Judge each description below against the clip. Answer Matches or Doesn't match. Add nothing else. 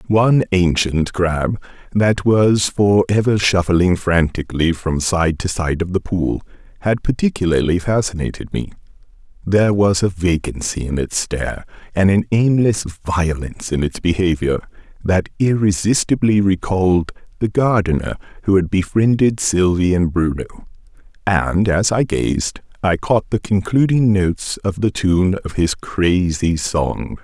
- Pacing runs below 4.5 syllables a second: Matches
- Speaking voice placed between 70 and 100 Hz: Matches